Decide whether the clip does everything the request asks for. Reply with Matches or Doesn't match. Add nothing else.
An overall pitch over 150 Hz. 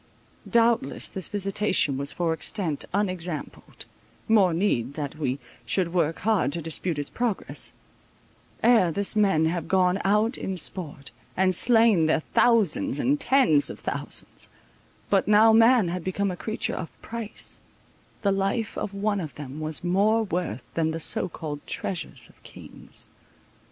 Matches